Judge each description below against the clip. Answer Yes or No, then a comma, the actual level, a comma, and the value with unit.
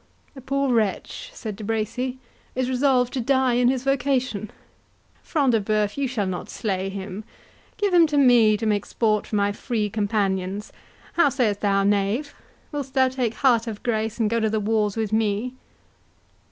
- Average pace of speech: Yes, average, 170 wpm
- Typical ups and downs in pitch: Yes, average, 3.9 semitones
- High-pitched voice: Yes, high, 225 Hz